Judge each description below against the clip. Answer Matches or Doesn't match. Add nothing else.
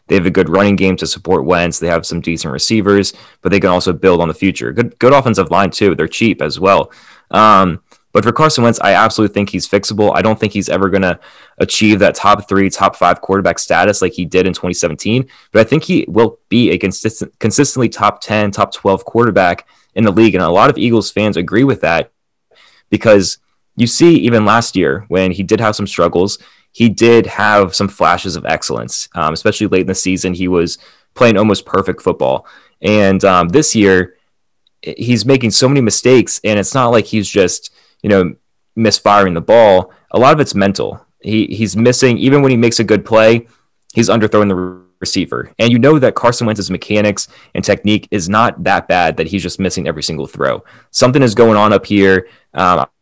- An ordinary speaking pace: Doesn't match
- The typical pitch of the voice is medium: Doesn't match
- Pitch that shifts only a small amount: Doesn't match